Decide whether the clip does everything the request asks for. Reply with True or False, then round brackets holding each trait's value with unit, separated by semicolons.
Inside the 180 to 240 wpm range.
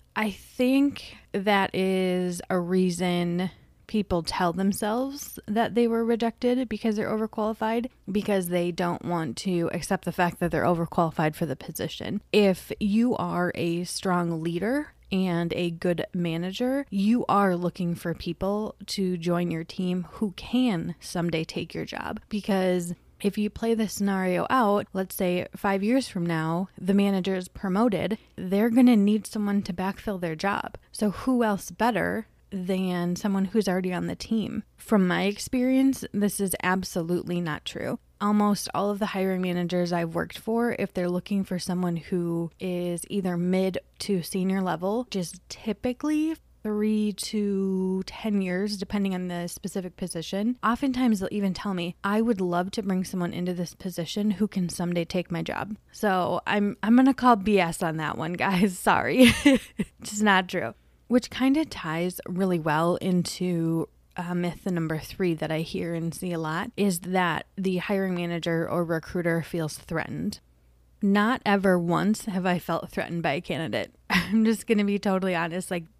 False (165 wpm)